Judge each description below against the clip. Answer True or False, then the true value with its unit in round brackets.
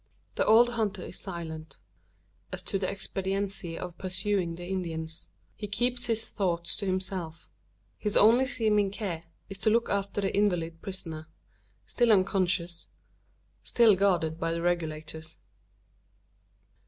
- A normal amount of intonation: True (3.5 semitones)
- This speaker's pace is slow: True (130 wpm)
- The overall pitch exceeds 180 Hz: True (190 Hz)